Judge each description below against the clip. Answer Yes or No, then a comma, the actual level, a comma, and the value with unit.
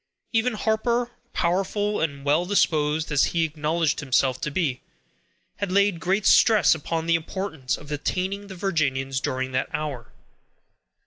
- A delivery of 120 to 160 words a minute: Yes, average, 140 wpm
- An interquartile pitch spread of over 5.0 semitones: Yes, wide, 5.4 semitones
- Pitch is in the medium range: Yes, medium, 165 Hz